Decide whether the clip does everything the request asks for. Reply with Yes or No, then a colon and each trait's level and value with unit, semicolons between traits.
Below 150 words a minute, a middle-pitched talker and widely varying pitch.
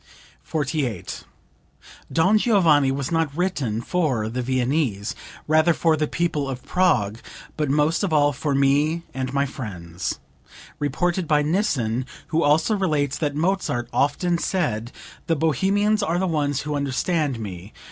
No: average, 140 wpm; medium, 150 Hz; average, 4.4 semitones